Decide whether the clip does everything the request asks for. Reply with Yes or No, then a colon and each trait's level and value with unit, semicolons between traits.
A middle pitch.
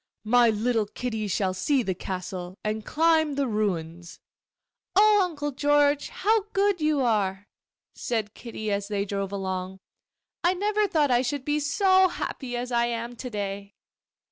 No: high, 240 Hz